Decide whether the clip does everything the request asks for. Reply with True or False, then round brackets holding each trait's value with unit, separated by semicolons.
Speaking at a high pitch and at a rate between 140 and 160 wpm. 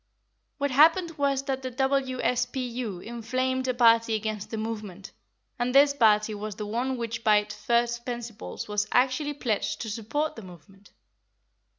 True (235 Hz; 155 wpm)